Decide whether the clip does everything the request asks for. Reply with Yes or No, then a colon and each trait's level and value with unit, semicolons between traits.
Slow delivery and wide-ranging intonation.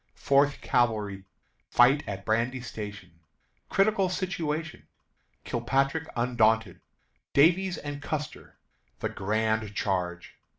Yes: slow, 90 wpm; wide, 5.8 semitones